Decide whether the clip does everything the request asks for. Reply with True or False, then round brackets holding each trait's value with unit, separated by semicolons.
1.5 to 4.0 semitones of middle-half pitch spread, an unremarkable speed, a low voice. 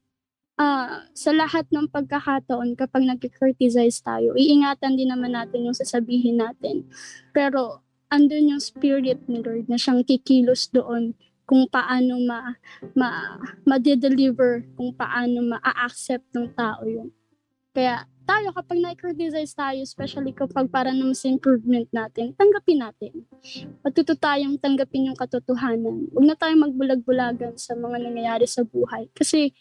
False (2.6 semitones; 130 wpm; 260 Hz)